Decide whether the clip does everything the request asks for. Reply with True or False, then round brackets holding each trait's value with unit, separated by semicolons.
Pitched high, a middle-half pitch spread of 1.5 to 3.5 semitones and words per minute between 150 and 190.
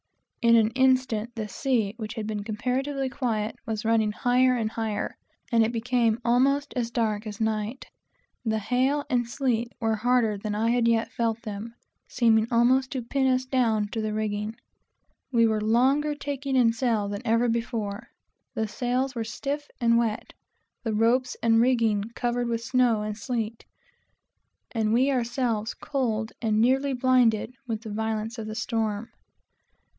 True (230 Hz; 2.5 semitones; 165 wpm)